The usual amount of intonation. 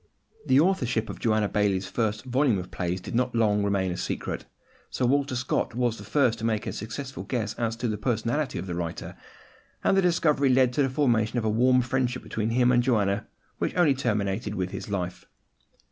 Yes: average, 3.7 semitones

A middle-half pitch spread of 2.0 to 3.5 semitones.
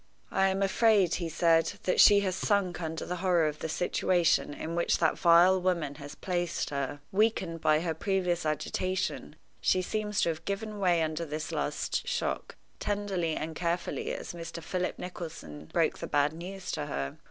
Yes: average, 2.9 semitones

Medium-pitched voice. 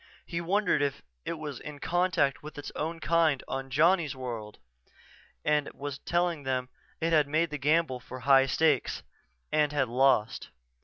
Yes: medium, 145 Hz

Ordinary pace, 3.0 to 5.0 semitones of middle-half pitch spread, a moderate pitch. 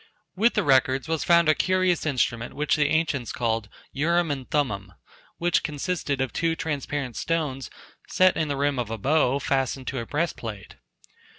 Yes: average, 170 wpm; average, 4.1 semitones; medium, 145 Hz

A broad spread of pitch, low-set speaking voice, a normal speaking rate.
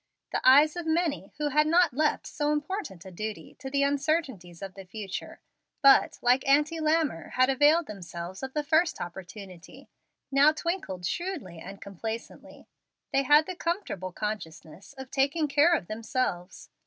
No: wide, 7.9 semitones; very high, 270 Hz; average, 155 wpm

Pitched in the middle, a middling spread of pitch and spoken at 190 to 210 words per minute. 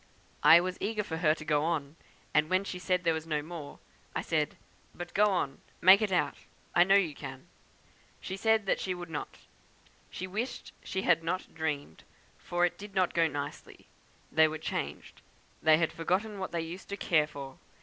Yes: medium, 170 Hz; average, 3.2 semitones; average, 195 wpm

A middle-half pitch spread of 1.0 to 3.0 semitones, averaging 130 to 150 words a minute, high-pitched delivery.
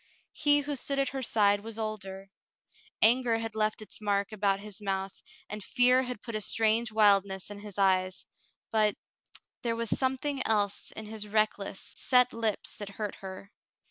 No: narrow, 2.5 semitones; average, 175 wpm; high, 215 Hz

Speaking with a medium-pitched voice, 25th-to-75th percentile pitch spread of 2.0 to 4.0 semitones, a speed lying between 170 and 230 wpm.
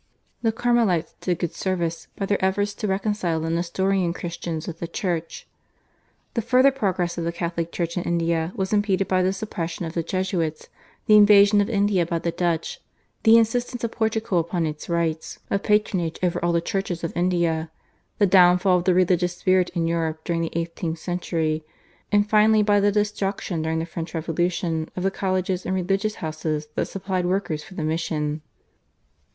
Yes: medium, 180 Hz; average, 3.1 semitones; average, 180 wpm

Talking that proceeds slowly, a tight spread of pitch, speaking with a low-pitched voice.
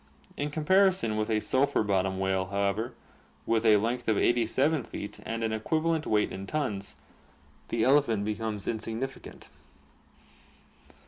No: slow, 130 wpm; average, 4.5 semitones; low, 110 Hz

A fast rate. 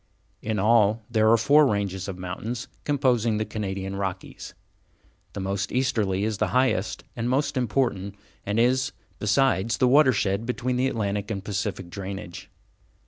No: average, 145 wpm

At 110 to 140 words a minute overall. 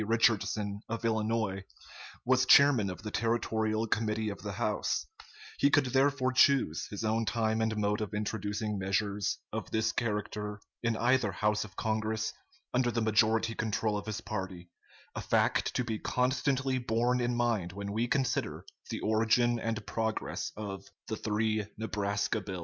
No: average, 155 wpm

